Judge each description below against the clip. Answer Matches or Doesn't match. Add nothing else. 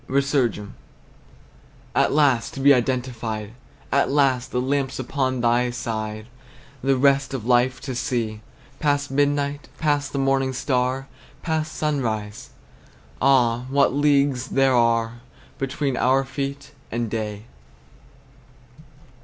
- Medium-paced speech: Doesn't match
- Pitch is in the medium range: Doesn't match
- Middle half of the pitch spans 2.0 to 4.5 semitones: Matches